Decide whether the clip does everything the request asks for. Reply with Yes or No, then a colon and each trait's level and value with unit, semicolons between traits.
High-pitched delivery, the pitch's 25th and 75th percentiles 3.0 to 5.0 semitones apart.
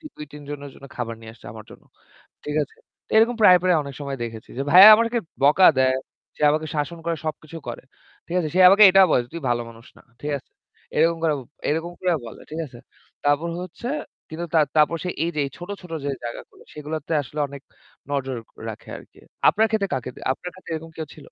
No: medium, 155 Hz; average, 4.0 semitones